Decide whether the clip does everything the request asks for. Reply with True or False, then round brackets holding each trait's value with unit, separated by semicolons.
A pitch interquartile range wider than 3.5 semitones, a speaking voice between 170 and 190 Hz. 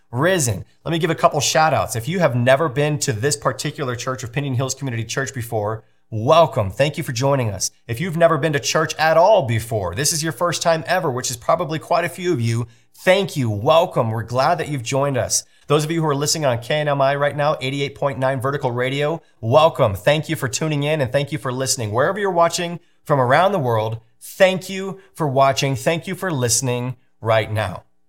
False (4.5 semitones; 140 Hz)